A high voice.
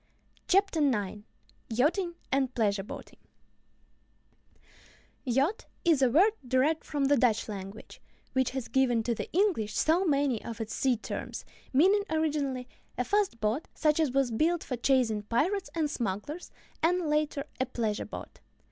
Yes: very high, 270 Hz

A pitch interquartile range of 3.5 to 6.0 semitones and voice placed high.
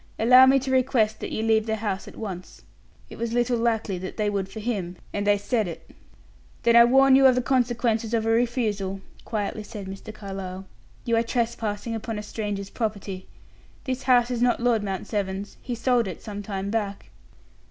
No: average, 3.0 semitones; high, 220 Hz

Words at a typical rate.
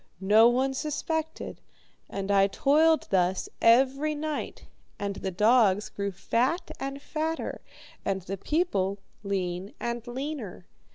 No: slow, 120 wpm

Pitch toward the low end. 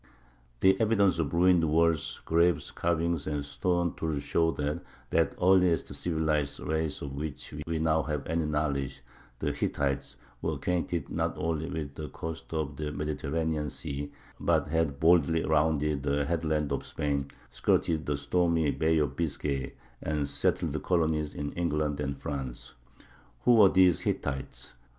Yes: very low, 75 Hz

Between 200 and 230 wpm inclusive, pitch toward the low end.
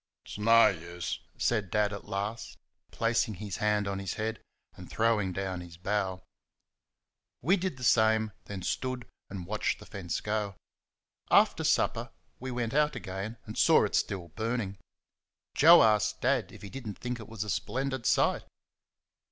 No: average, 165 wpm; low, 105 Hz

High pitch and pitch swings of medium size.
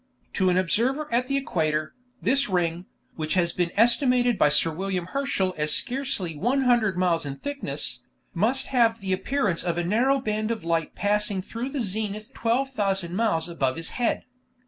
No: high, 205 Hz; wide, 6.3 semitones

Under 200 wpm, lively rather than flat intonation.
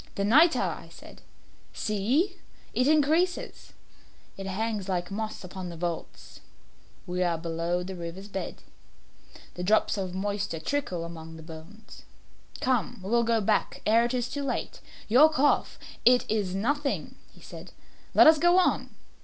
Yes: average, 155 wpm; wide, 6.5 semitones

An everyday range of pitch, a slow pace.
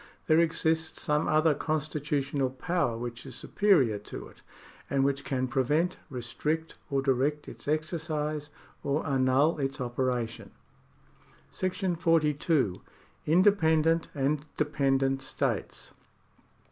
Yes: average, 3.2 semitones; slow, 110 wpm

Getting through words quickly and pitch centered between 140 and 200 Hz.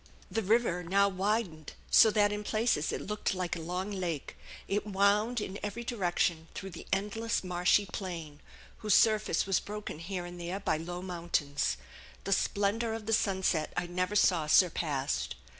No: average, 165 wpm; high, 190 Hz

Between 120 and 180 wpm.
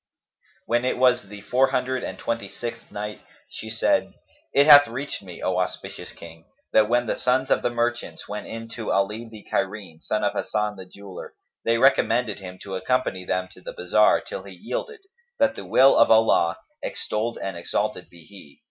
No: average, 190 wpm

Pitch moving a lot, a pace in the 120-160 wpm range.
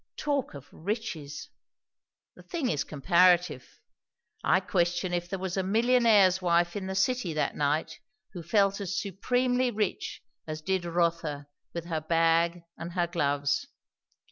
No: average, 3.2 semitones; average, 140 wpm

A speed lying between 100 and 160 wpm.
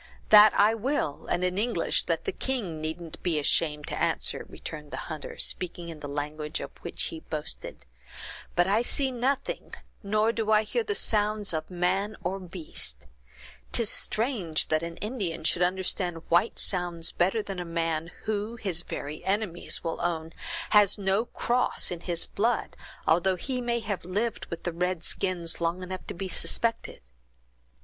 No: average, 170 wpm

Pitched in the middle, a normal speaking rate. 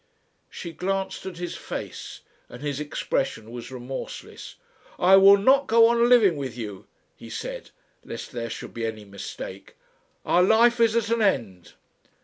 Yes: medium, 175 Hz; average, 155 wpm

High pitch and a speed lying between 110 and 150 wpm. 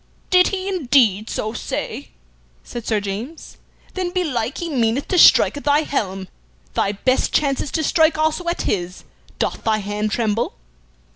No: very high, 255 Hz; average, 160 wpm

